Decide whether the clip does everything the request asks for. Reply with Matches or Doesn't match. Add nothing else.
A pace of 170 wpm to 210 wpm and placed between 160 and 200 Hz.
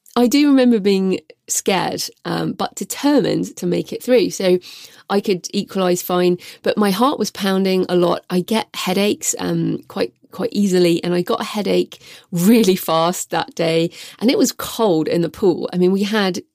Matches